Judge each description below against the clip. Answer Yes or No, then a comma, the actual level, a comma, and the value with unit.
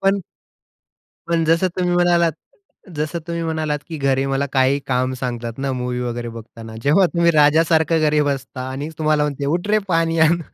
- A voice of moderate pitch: Yes, medium, 150 Hz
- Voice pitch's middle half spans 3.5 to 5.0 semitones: Yes, average, 3.8 semitones